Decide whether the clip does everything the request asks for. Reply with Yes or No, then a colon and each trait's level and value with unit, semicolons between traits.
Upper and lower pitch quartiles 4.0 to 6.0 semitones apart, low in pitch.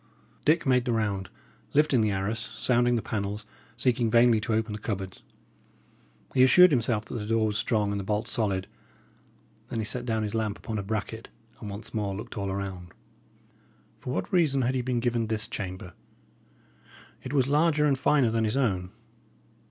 No: average, 3.2 semitones; low, 110 Hz